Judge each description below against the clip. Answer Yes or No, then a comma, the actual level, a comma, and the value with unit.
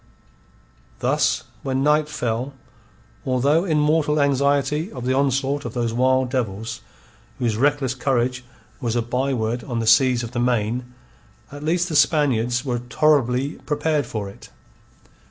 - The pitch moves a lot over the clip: No, average, 3.2 semitones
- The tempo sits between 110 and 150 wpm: Yes, average, 140 wpm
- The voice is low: Yes, low, 130 Hz